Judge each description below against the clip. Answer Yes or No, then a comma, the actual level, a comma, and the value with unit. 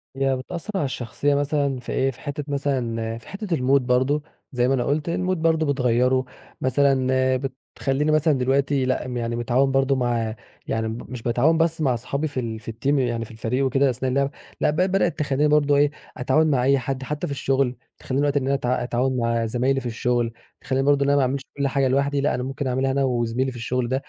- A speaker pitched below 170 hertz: Yes, low, 135 Hz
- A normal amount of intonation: No, narrow, 2.3 semitones